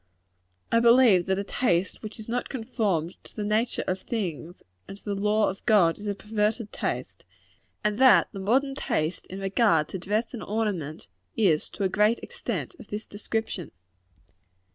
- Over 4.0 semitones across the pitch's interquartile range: No, average, 2.9 semitones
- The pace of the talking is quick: No, average, 175 wpm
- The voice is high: Yes, high, 210 Hz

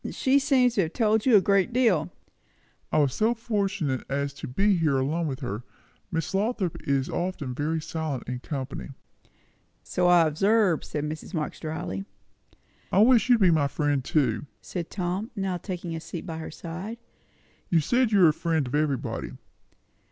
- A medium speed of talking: Yes, average, 175 wpm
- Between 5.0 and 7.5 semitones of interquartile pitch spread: Yes, wide, 5.5 semitones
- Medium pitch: Yes, medium, 165 Hz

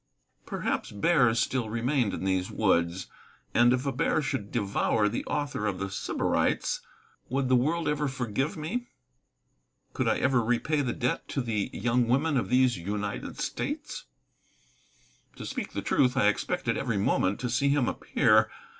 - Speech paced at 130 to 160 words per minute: Yes, average, 155 wpm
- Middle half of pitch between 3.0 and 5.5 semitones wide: Yes, average, 4.6 semitones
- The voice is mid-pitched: No, low, 125 Hz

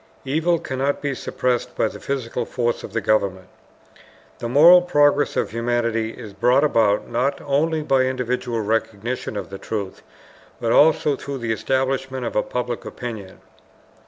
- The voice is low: Yes, low, 125 Hz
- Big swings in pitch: No, average, 3.5 semitones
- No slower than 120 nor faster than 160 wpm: Yes, average, 150 wpm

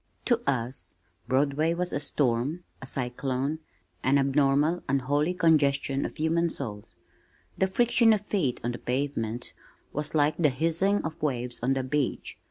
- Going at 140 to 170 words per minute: Yes, average, 150 wpm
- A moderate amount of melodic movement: Yes, average, 3.9 semitones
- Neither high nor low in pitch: Yes, medium, 145 Hz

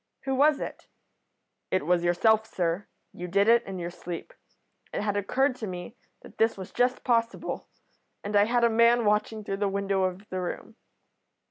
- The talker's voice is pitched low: No, high, 205 Hz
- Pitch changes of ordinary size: Yes, average, 3.8 semitones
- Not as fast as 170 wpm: No, average, 185 wpm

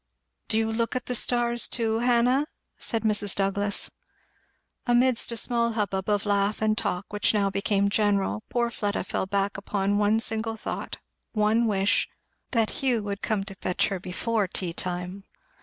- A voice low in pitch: No, high, 210 Hz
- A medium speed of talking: Yes, average, 170 wpm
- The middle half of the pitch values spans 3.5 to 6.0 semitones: No, narrow, 2.6 semitones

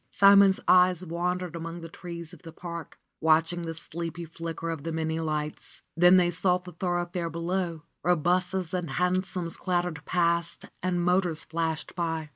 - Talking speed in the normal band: Yes, average, 160 wpm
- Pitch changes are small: Yes, narrow, 1.7 semitones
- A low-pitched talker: No, medium, 170 Hz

